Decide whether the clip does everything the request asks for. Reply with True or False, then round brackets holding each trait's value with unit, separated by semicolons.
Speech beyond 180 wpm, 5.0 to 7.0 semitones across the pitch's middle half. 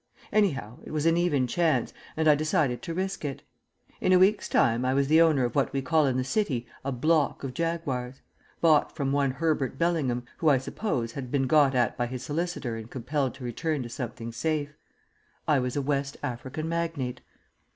False (200 wpm; 4.1 semitones)